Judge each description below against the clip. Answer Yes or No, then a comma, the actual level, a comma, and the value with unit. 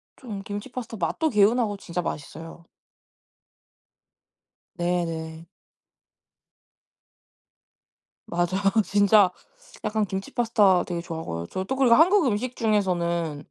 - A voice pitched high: Yes, high, 195 Hz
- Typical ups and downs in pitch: Yes, average, 4.8 semitones